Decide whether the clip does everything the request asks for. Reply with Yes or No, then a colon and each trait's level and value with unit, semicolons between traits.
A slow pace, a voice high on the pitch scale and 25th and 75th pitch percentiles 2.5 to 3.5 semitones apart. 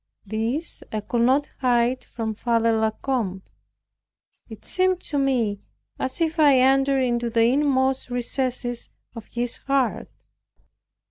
Yes: slow, 130 wpm; high, 245 Hz; average, 2.9 semitones